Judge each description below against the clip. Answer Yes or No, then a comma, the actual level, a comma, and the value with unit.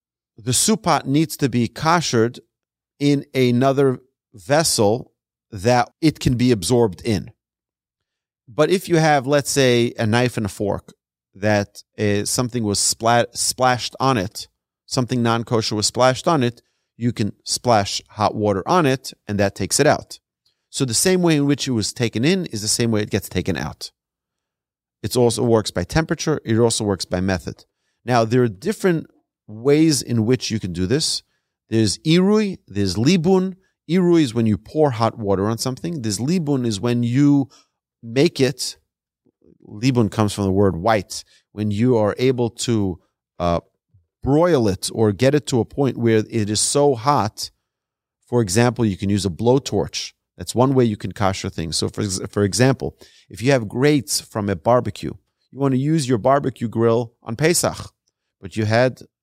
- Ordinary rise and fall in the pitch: Yes, average, 4.4 semitones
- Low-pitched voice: Yes, low, 120 Hz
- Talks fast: No, average, 175 wpm